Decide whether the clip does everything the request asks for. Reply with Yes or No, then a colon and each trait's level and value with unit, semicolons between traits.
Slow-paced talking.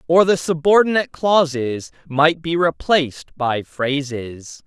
Yes: slow, 115 wpm